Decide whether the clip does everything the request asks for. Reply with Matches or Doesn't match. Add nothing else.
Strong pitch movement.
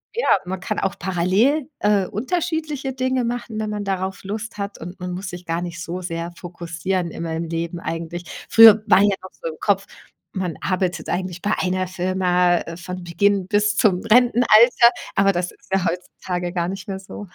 Doesn't match